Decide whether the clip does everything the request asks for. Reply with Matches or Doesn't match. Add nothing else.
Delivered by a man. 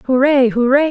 Doesn't match